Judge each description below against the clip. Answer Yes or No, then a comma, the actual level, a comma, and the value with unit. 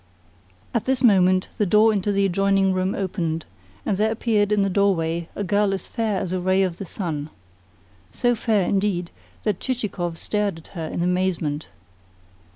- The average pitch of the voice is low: No, high, 195 Hz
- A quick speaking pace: No, average, 170 wpm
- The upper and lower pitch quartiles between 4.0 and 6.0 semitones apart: No, average, 2.8 semitones